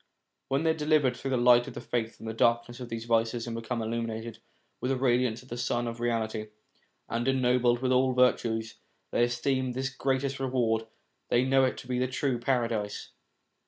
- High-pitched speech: No, low, 120 Hz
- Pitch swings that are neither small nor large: No, narrow, 2.0 semitones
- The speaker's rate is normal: No, fast, 210 wpm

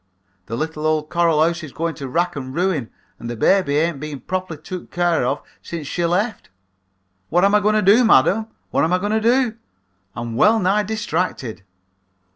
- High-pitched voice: No, medium, 170 Hz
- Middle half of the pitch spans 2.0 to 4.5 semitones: No, average, 5.0 semitones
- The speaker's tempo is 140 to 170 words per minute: No, average, 195 wpm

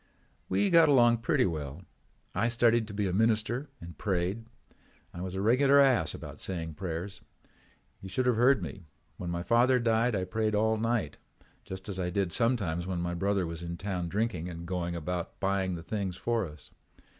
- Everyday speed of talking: Yes, average, 190 wpm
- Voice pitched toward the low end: Yes, low, 100 Hz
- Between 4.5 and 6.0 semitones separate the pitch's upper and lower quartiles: Yes, average, 4.8 semitones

